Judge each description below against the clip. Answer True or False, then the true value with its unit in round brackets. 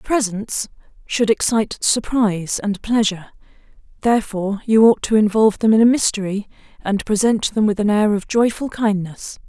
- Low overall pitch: False (215 Hz)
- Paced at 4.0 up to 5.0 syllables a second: False (5.2 syllables/s)